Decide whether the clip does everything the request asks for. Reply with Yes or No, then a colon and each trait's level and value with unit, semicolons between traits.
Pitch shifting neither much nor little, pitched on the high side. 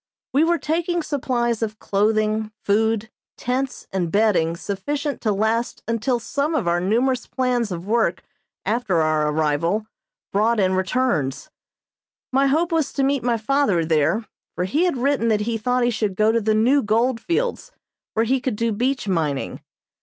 Yes: average, 4.6 semitones; high, 225 Hz